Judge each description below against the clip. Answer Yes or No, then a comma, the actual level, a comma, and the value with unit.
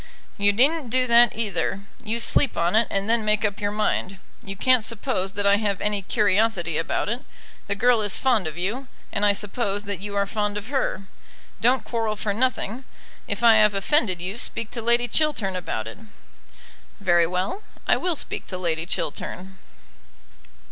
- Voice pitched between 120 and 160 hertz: No, high, 210 Hz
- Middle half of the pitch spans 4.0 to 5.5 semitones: No, average, 3.2 semitones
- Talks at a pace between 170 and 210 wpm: Yes, average, 180 wpm